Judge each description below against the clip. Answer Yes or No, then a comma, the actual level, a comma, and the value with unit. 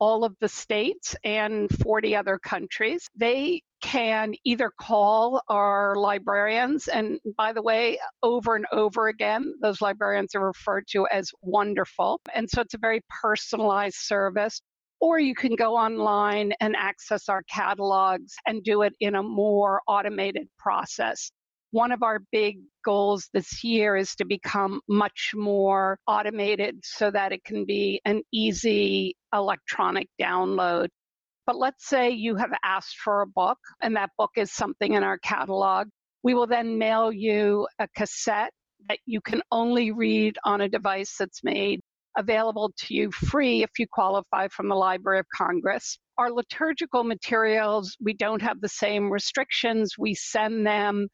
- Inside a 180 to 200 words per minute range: No, average, 155 wpm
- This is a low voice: No, high, 210 Hz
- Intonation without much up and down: Yes, narrow, 2.0 semitones